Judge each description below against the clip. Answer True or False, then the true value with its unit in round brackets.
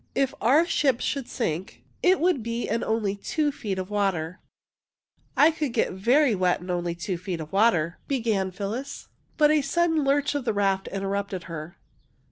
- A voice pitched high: True (215 Hz)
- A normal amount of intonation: False (6.9 semitones)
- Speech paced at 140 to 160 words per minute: False (180 wpm)